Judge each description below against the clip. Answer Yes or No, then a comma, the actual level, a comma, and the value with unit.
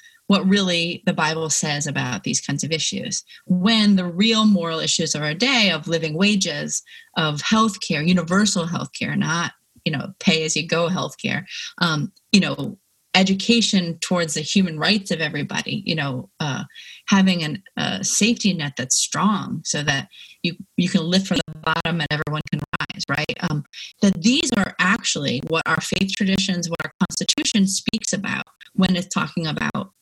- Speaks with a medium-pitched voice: Yes, medium, 180 Hz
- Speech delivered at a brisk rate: No, average, 175 wpm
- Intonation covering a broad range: No, average, 3.8 semitones